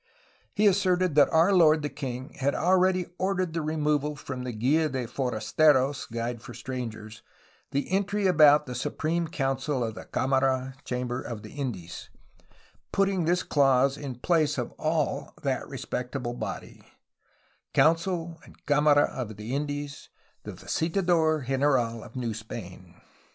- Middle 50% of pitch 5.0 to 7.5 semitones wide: No, average, 4.4 semitones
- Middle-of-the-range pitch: Yes, medium, 145 Hz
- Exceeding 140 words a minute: Yes, average, 150 wpm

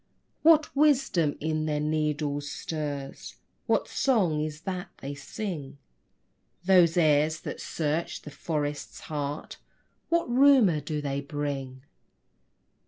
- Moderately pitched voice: Yes, medium, 155 Hz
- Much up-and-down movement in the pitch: No, average, 3.8 semitones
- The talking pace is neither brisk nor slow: No, slow, 110 wpm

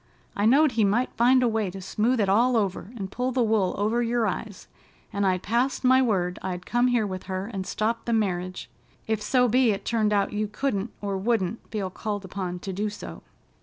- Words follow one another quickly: Yes, fast, 215 wpm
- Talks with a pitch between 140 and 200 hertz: No, high, 215 Hz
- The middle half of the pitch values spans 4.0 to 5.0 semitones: No, average, 3.6 semitones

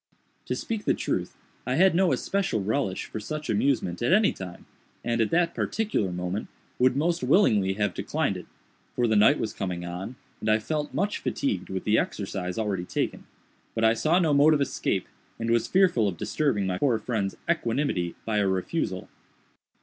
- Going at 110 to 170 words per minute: No, average, 185 wpm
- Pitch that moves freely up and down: Yes, wide, 7.9 semitones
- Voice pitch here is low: Yes, low, 115 Hz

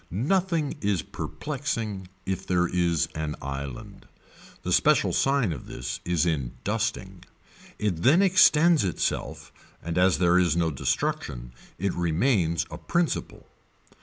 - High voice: No, very low, 90 Hz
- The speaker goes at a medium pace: No, slow, 130 wpm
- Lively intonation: Yes, wide, 8.8 semitones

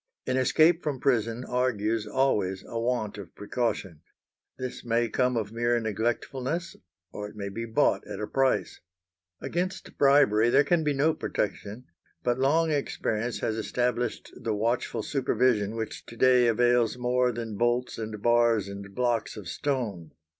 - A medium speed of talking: Yes, average, 155 wpm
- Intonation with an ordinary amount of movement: Yes, average, 3.0 semitones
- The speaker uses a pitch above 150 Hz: No, low, 120 Hz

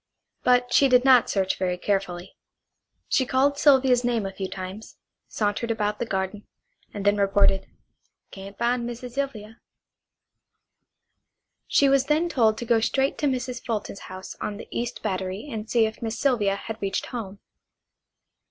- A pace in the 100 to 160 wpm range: Yes, average, 155 wpm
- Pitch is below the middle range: No, high, 225 Hz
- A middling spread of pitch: Yes, average, 4.0 semitones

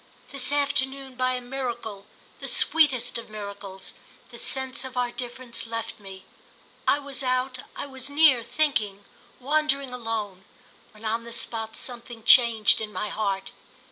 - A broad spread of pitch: No, average, 3.3 semitones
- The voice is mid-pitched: No, high, 245 Hz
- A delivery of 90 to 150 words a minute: Yes, average, 140 wpm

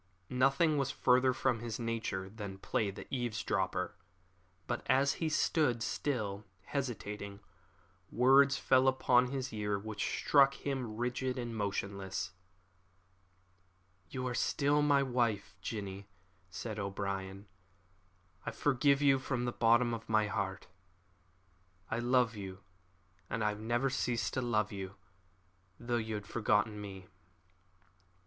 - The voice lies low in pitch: Yes, low, 120 Hz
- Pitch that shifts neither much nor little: Yes, average, 4.0 semitones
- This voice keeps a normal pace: No, slow, 125 wpm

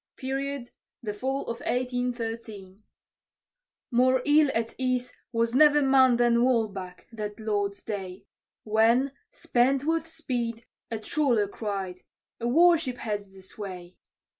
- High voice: Yes, high, 235 Hz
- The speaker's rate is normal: No, slow, 125 wpm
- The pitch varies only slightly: No, average, 3.9 semitones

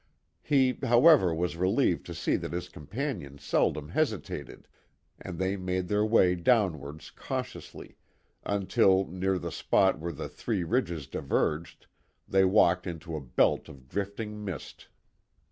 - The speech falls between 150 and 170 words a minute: No, slow, 135 wpm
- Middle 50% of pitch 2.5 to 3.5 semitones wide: No, average, 4.0 semitones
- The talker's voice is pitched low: Yes, very low, 95 Hz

